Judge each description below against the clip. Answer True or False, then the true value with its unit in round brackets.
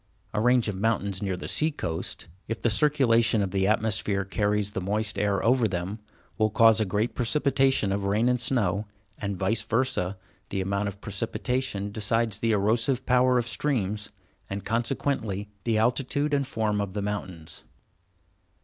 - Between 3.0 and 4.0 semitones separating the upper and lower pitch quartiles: True (3.4 semitones)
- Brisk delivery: False (165 wpm)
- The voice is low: True (110 Hz)